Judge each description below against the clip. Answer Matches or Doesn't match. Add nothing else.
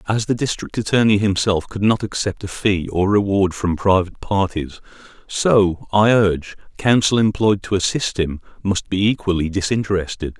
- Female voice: Doesn't match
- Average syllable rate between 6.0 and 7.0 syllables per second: Doesn't match